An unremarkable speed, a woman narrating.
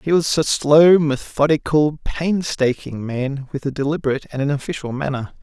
No: average, 155 wpm; male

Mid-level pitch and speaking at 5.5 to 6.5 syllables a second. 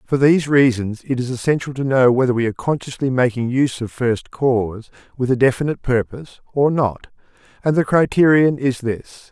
No: low, 130 Hz; 5.6 syllables/s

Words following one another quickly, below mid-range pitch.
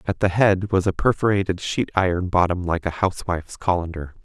No: average, 185 wpm; very low, 90 Hz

